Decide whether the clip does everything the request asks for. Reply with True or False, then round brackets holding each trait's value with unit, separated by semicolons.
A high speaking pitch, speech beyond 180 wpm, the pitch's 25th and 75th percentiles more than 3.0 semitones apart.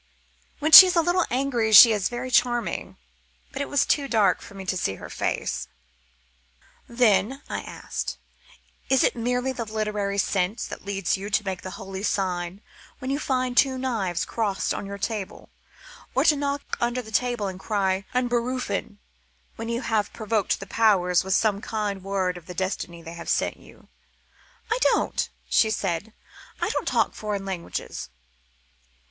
False (215 Hz; 170 wpm; 4.2 semitones)